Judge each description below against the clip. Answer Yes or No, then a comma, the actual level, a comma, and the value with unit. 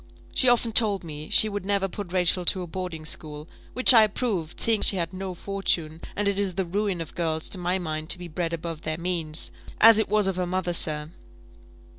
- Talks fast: Yes, fast, 220 wpm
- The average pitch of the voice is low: No, medium, 180 Hz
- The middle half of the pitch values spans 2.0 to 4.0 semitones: Yes, average, 3.4 semitones